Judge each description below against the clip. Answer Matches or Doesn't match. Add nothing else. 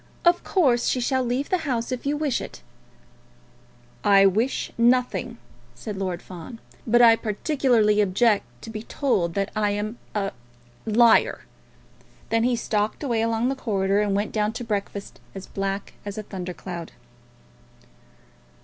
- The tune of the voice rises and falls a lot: Doesn't match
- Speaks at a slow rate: Doesn't match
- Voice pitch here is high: Matches